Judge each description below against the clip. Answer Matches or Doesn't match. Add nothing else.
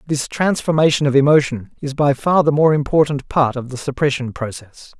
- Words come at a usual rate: Matches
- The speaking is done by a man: Matches